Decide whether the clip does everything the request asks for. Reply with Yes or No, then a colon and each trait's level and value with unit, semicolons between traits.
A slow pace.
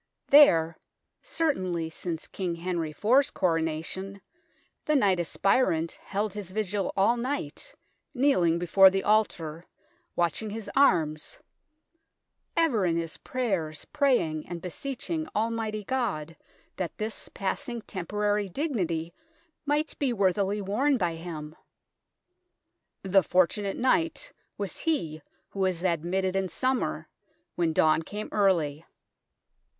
Yes: slow, 115 wpm